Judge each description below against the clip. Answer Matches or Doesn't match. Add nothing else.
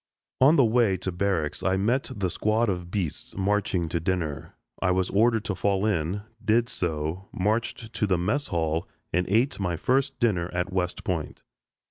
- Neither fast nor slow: Matches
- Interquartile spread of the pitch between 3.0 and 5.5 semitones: Matches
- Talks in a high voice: Doesn't match